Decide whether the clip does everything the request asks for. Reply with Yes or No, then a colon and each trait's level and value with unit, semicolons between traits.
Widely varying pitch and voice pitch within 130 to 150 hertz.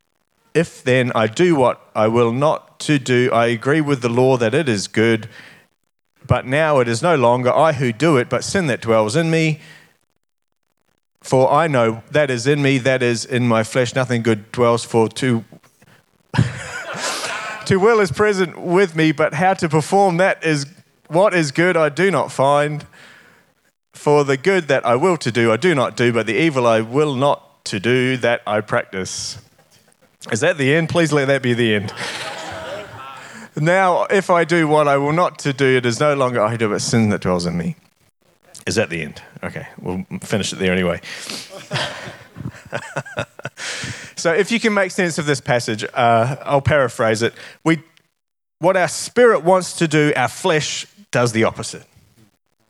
Yes: wide, 5.9 semitones; medium, 140 Hz